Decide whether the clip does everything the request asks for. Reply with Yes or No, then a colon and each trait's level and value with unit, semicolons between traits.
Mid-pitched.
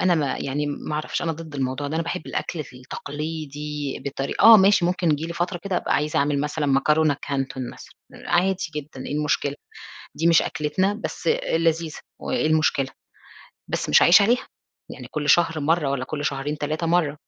Yes: medium, 150 Hz